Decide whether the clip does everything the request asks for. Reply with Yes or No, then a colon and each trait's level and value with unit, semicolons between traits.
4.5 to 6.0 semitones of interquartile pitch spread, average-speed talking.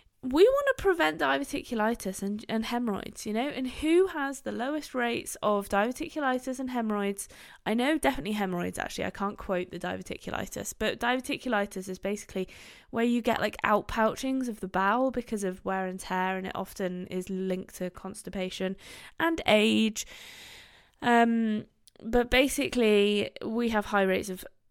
Yes: average, 4.8 semitones; average, 160 wpm